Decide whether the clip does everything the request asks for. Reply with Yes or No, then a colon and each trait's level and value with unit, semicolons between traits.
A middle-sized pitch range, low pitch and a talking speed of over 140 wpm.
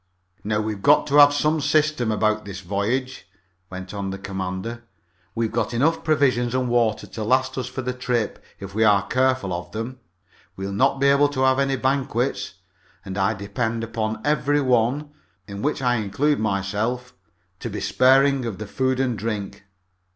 Yes: average, 4.4 semitones; low, 120 Hz; average, 175 wpm